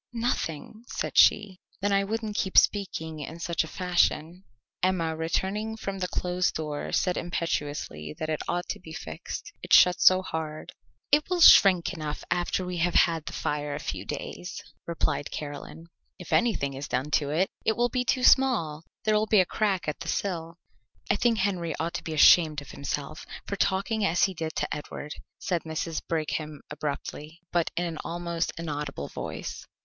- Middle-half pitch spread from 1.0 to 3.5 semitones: No, average, 4.0 semitones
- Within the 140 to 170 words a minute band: No, average, 180 wpm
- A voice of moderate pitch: Yes, medium, 170 Hz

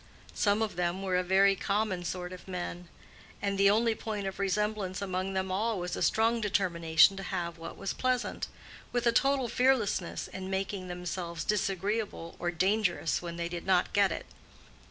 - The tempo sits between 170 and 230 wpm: Yes, average, 175 wpm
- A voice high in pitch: Yes, high, 195 Hz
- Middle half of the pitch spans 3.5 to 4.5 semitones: No, average, 2.9 semitones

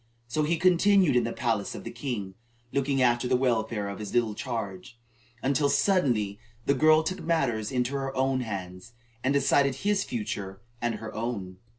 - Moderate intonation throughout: Yes, average, 4.4 semitones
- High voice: No, low, 125 Hz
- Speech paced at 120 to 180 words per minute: Yes, average, 175 wpm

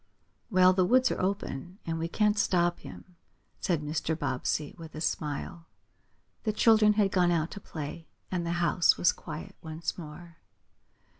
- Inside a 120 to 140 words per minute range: No, average, 160 wpm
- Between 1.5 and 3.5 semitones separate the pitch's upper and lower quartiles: Yes, average, 2.7 semitones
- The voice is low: No, medium, 170 Hz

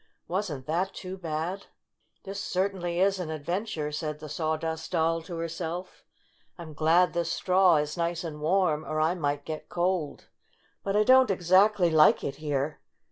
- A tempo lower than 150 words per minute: No, average, 170 wpm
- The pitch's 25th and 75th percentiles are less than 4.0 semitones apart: Yes, average, 3.0 semitones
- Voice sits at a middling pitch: Yes, medium, 170 Hz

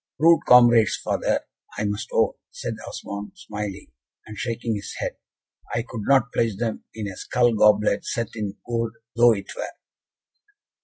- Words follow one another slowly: No, average, 155 wpm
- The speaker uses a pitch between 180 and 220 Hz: No, low, 110 Hz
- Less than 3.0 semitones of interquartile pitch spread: Yes, narrow, 2.5 semitones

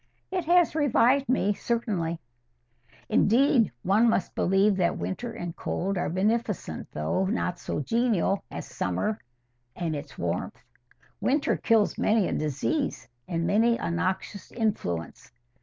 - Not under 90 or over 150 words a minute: Yes, slow, 135 wpm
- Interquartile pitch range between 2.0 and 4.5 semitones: No, wide, 5.5 semitones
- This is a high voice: Yes, high, 200 Hz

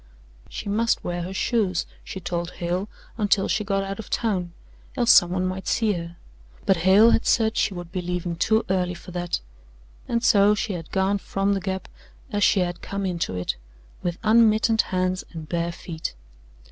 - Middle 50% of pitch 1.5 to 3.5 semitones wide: Yes, average, 2.9 semitones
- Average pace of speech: Yes, average, 185 wpm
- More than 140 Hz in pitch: Yes, high, 190 Hz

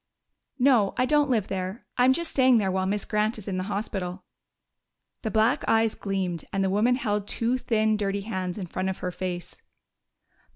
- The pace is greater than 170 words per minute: Yes, average, 190 wpm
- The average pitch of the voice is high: Yes, high, 210 Hz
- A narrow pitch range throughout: No, average, 3.5 semitones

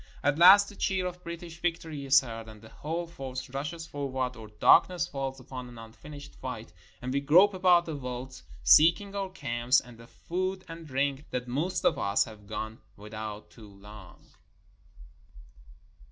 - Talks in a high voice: No, medium, 140 Hz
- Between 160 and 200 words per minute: Yes, average, 170 wpm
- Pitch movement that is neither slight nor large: No, wide, 6.2 semitones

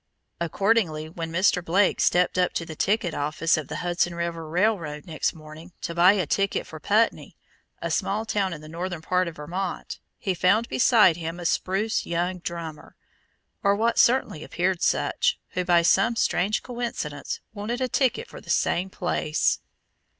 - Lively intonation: No, average, 3.7 semitones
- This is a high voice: No, medium, 180 Hz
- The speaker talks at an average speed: Yes, average, 170 wpm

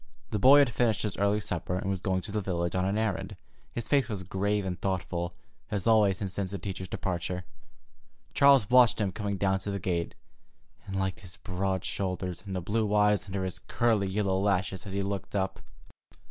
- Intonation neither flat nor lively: No, narrow, 2.0 semitones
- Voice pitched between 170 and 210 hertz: No, very low, 95 Hz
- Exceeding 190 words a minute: Yes, average, 200 wpm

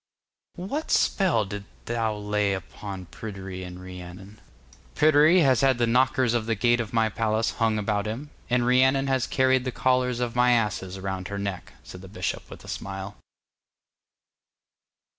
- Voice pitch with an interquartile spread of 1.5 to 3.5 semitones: No, average, 4.3 semitones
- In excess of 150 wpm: Yes, average, 160 wpm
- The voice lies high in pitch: No, low, 115 Hz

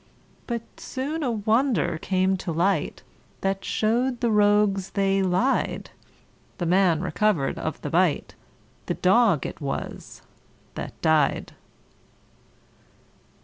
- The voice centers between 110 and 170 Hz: No, high, 195 Hz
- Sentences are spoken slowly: Yes, slow, 110 wpm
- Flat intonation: No, average, 4.2 semitones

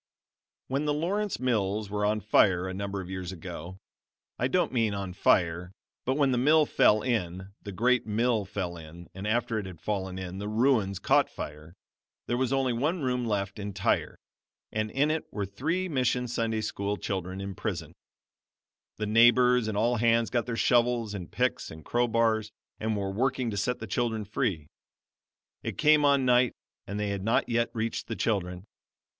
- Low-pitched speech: Yes, low, 110 Hz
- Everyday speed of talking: Yes, average, 180 wpm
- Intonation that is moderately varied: Yes, average, 4.3 semitones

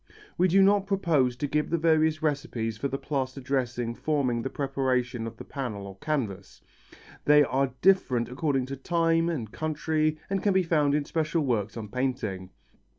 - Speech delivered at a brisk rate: No, average, 175 wpm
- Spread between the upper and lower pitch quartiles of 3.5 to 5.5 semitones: Yes, average, 4.2 semitones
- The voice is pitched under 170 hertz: Yes, medium, 140 Hz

